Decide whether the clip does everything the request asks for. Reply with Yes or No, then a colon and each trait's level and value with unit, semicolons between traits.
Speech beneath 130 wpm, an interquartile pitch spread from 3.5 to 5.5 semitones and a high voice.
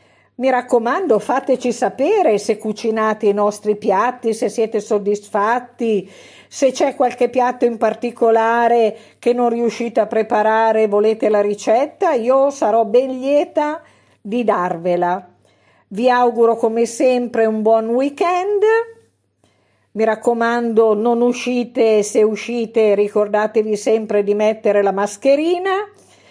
No: average, 120 wpm; average, 2.7 semitones; high, 230 Hz